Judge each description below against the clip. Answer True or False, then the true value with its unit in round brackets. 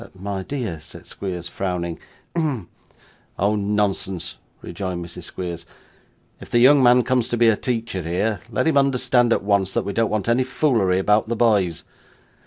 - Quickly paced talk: False (170 wpm)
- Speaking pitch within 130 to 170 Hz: False (105 Hz)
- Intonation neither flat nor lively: True (4.6 semitones)